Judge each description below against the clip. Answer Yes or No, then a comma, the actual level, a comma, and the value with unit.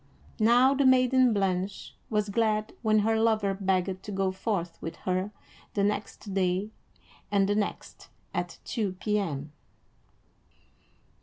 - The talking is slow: Yes, slow, 130 wpm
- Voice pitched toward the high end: Yes, high, 205 Hz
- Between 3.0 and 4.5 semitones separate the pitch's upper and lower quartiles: No, narrow, 2.6 semitones